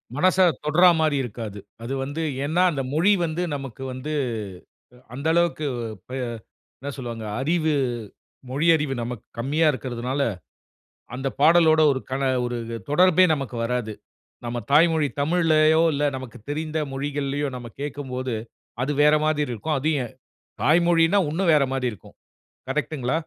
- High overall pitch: No, medium, 145 Hz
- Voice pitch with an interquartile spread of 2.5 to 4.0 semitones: Yes, average, 3.5 semitones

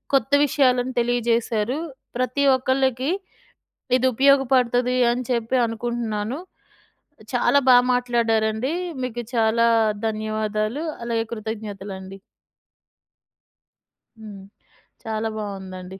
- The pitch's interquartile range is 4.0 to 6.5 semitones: No, narrow, 2.6 semitones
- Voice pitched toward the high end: Yes, high, 235 Hz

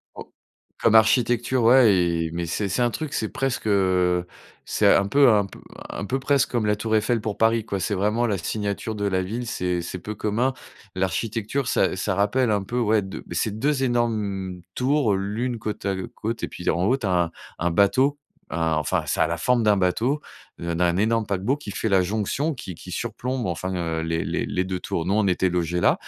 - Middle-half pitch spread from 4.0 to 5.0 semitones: Yes, average, 4.4 semitones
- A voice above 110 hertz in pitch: No, low, 105 Hz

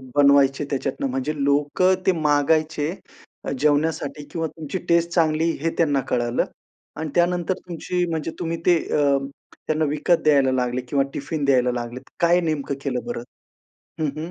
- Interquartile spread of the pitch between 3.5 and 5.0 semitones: No, average, 3.1 semitones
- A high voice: No, medium, 150 Hz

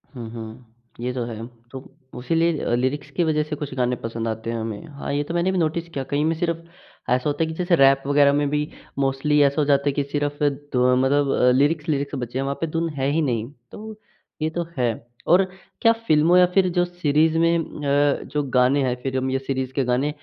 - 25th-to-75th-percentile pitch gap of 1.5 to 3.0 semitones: No, average, 3.5 semitones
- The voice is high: No, medium, 145 Hz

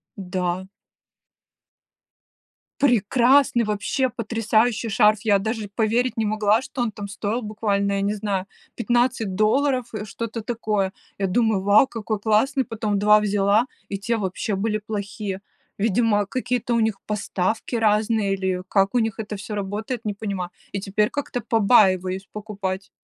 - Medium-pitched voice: No, high, 210 Hz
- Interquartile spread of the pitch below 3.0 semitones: Yes, narrow, 2.4 semitones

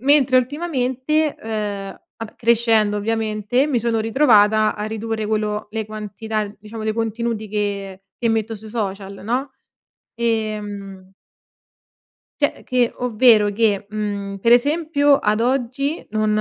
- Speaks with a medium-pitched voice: No, high, 220 Hz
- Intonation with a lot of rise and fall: No, narrow, 2.6 semitones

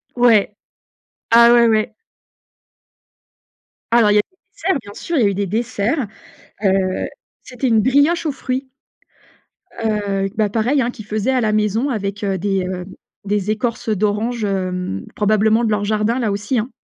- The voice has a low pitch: No, high, 215 Hz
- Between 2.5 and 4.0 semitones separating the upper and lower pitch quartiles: Yes, average, 2.9 semitones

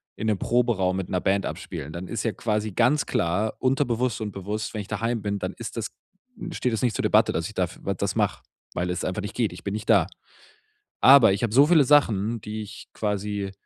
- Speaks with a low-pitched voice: Yes, low, 105 Hz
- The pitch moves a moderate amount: Yes, average, 3.1 semitones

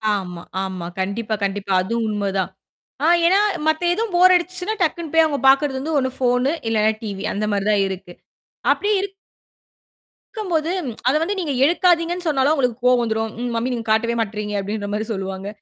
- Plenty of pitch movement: Yes, wide, 7.8 semitones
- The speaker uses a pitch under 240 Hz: No, high, 245 Hz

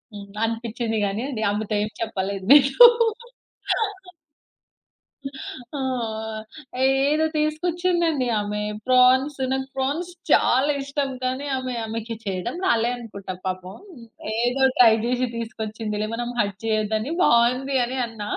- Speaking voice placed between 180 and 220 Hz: No, high, 240 Hz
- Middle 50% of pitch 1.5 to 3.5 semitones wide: No, average, 3.9 semitones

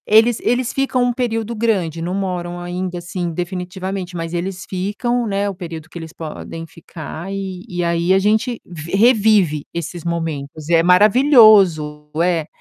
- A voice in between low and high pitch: Yes, medium, 180 Hz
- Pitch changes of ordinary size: Yes, average, 3.8 semitones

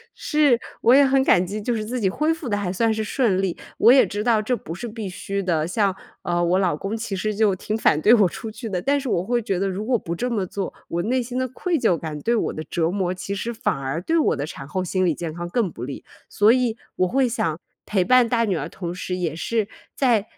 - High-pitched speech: Yes, high, 205 Hz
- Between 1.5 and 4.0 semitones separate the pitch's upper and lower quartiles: No, average, 5.0 semitones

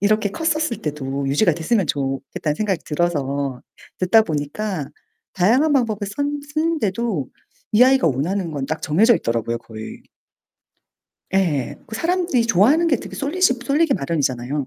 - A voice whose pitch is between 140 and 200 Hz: Yes, medium, 185 Hz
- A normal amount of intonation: No, wide, 8.9 semitones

